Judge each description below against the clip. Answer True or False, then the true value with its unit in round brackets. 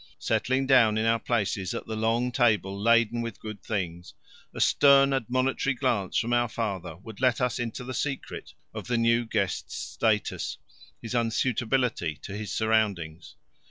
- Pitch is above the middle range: False (115 Hz)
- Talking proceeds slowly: False (160 wpm)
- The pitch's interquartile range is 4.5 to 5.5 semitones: False (3.3 semitones)